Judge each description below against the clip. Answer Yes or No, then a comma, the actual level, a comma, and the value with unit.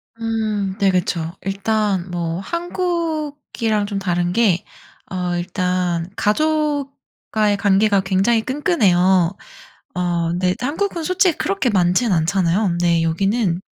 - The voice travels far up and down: No, average, 4.8 semitones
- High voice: Yes, high, 195 Hz